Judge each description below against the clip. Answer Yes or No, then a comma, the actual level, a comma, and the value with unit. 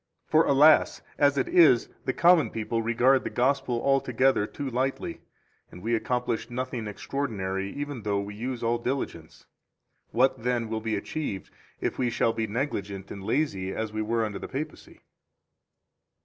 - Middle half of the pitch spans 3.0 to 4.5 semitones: Yes, average, 3.9 semitones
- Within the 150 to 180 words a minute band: Yes, average, 165 wpm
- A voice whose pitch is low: Yes, low, 120 Hz